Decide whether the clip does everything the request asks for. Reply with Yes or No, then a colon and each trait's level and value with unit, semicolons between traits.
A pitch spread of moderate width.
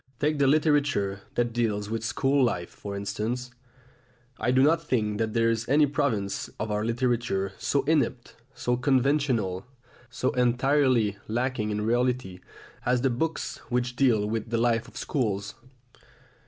Yes: average, 3.8 semitones